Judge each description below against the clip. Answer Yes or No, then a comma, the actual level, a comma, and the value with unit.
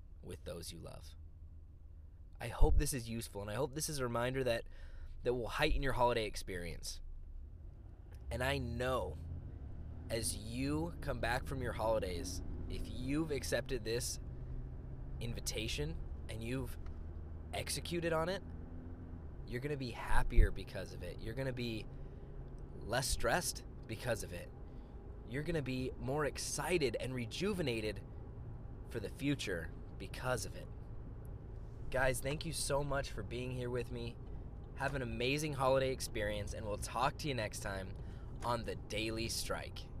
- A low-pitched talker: Yes, low, 110 Hz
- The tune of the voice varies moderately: No, wide, 6.8 semitones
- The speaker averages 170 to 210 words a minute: No, average, 150 wpm